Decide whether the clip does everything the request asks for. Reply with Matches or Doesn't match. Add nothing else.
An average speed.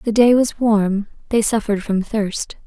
Matches